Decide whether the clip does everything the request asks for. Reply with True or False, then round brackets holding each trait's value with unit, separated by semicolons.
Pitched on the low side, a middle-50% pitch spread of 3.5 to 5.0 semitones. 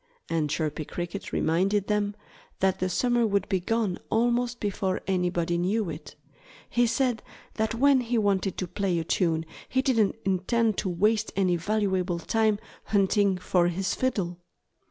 False (195 Hz; 3.9 semitones)